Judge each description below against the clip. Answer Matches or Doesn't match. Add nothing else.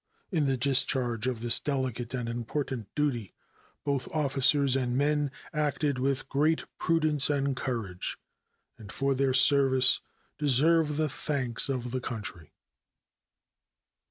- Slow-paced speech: Matches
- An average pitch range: Matches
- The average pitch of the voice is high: Doesn't match